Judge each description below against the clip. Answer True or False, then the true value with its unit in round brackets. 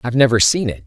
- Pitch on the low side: True (120 Hz)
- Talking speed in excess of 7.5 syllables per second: True (7.8 syllables/s)